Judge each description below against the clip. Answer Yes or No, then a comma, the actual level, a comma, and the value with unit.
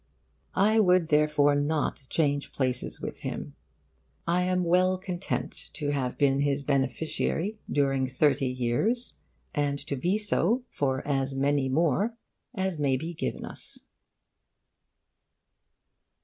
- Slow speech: Yes, slow, 120 wpm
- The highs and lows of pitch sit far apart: No, average, 4.8 semitones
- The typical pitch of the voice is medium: Yes, medium, 145 Hz